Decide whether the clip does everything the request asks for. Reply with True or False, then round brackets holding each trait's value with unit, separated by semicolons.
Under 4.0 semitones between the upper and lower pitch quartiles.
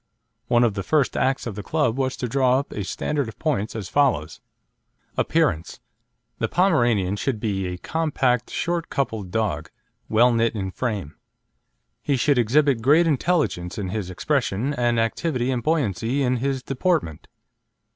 False (5.1 semitones)